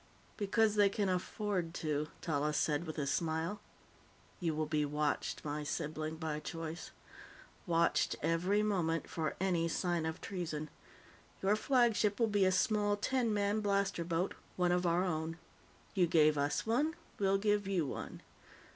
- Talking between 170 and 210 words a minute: No, average, 155 wpm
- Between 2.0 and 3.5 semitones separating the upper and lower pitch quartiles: No, average, 4.4 semitones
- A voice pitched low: No, medium, 175 Hz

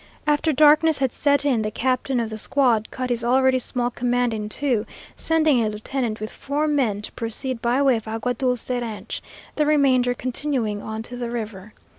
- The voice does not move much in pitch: No, average, 3.5 semitones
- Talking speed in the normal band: Yes, average, 190 wpm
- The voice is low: No, high, 245 Hz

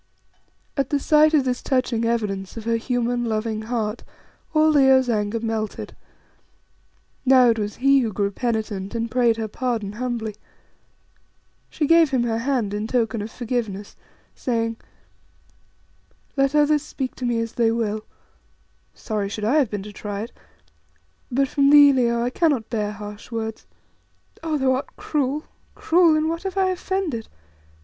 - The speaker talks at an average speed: Yes, average, 155 wpm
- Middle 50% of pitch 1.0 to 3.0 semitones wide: No, average, 3.9 semitones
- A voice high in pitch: Yes, high, 235 Hz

